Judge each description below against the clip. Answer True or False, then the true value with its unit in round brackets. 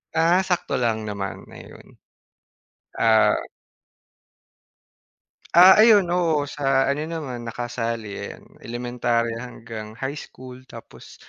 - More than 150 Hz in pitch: False (125 Hz)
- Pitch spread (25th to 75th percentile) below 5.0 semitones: False (5.3 semitones)